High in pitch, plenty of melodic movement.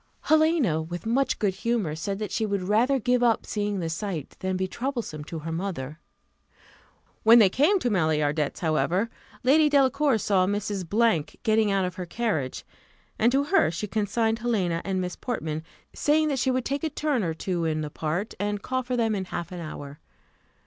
Yes: high, 205 Hz; wide, 6.1 semitones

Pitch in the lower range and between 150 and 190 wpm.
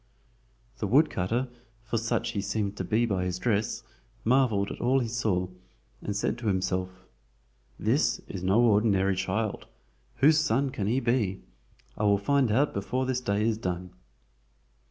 Yes: low, 110 Hz; average, 155 wpm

